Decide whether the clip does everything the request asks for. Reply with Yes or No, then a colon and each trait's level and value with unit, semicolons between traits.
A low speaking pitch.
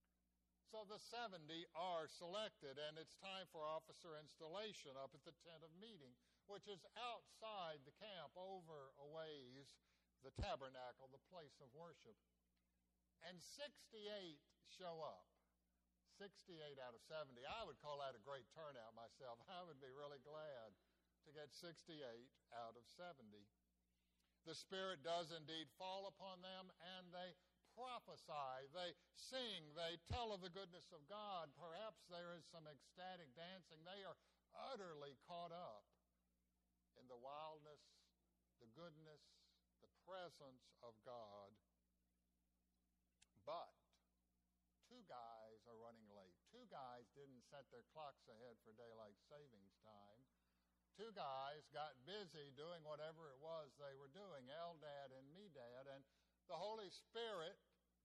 No: medium, 150 Hz